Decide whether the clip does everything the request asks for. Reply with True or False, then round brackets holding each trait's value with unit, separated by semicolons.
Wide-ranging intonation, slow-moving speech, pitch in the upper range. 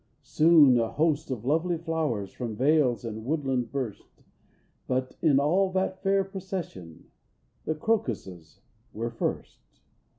False (6.1 semitones; 125 wpm; 140 Hz)